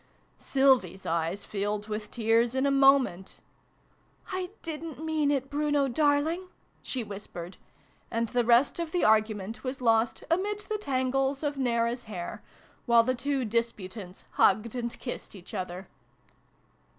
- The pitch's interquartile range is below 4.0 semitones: No, average, 4.9 semitones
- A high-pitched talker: Yes, high, 245 Hz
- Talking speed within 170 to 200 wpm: No, average, 150 wpm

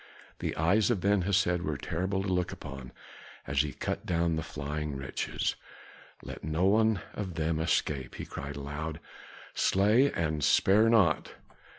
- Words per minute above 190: No, average, 155 wpm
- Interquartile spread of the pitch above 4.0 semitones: Yes, average, 4.5 semitones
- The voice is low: Yes, very low, 85 Hz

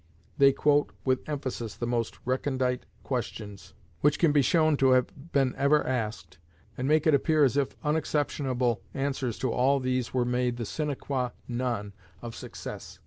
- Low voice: Yes, low, 130 Hz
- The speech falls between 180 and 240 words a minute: No, average, 165 wpm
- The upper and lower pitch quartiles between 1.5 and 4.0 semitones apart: Yes, average, 2.8 semitones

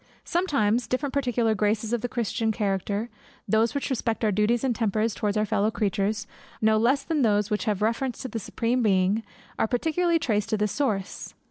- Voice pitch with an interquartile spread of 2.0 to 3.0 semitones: Yes, average, 2.7 semitones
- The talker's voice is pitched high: Yes, high, 220 Hz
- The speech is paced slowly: No, average, 190 wpm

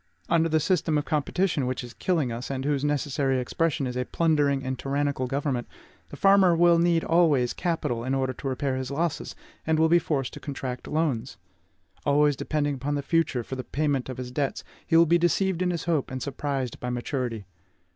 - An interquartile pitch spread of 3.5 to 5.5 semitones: Yes, average, 3.9 semitones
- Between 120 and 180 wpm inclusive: No, average, 200 wpm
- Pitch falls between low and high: Yes, medium, 145 Hz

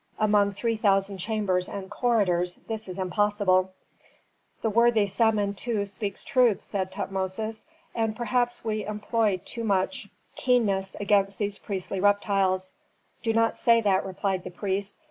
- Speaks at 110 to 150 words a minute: Yes, slow, 135 wpm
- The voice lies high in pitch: Yes, high, 205 Hz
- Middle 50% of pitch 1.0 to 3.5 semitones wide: Yes, narrow, 2.6 semitones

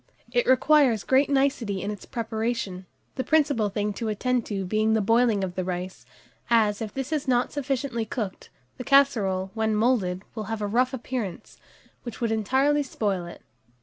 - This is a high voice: Yes, high, 225 Hz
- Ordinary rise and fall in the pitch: Yes, average, 4.1 semitones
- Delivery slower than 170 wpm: No, average, 175 wpm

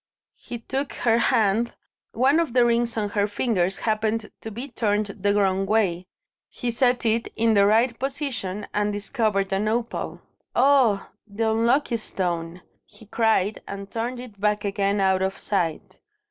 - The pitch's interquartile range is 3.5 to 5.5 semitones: No, average, 2.9 semitones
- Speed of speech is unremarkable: Yes, average, 160 wpm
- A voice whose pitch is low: No, high, 220 Hz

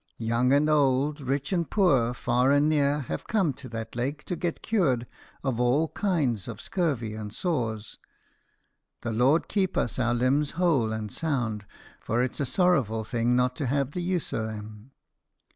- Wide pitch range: No, average, 4.6 semitones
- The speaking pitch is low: Yes, low, 130 Hz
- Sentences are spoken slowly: No, average, 175 wpm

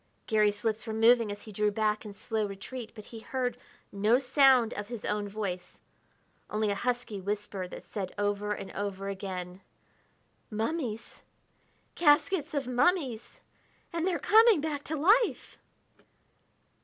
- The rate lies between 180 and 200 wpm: No, average, 145 wpm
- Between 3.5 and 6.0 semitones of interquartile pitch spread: Yes, average, 4.2 semitones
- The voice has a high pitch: Yes, high, 220 Hz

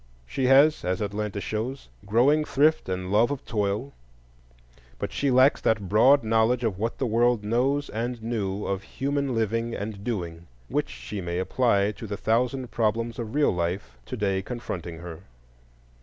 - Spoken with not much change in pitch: No, average, 4.0 semitones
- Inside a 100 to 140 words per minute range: No, average, 165 wpm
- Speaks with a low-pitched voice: Yes, low, 110 Hz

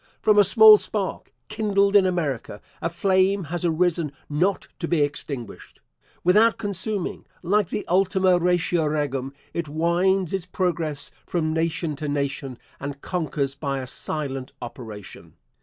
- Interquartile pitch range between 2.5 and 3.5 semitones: No, average, 4.6 semitones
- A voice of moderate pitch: Yes, medium, 170 Hz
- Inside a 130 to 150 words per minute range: Yes, average, 140 wpm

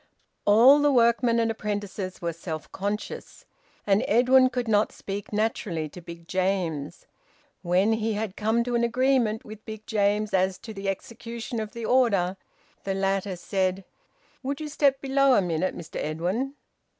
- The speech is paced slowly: No, average, 160 wpm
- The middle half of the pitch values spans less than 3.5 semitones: No, average, 3.9 semitones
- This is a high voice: Yes, high, 210 Hz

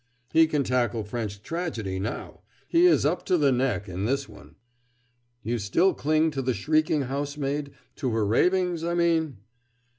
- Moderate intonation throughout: No, wide, 6.0 semitones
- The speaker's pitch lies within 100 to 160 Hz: Yes, medium, 140 Hz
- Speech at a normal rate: Yes, average, 160 wpm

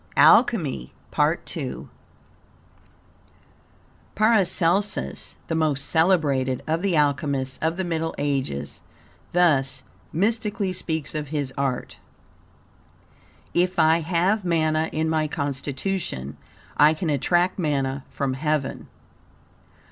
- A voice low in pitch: No, medium, 155 Hz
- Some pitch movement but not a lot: Yes, average, 4.2 semitones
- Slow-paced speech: Yes, slow, 100 wpm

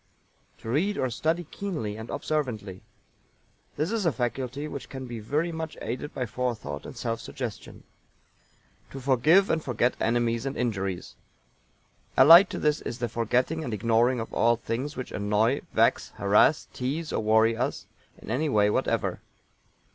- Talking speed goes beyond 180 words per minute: No, average, 155 wpm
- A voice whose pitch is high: No, low, 125 Hz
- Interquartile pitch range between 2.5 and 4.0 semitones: No, average, 4.7 semitones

